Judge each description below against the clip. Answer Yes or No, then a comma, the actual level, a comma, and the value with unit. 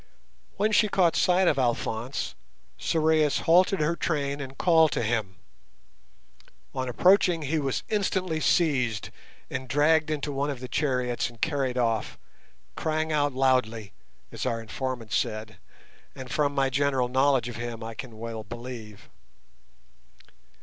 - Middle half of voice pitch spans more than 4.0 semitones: Yes, average, 4.7 semitones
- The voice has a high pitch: No, low, 135 Hz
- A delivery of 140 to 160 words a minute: Yes, average, 145 wpm